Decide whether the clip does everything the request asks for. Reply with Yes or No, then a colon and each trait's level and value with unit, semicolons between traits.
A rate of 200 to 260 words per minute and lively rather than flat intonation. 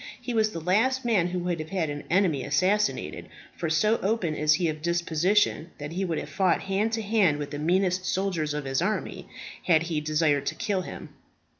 No: fast, 205 wpm; average, 4.2 semitones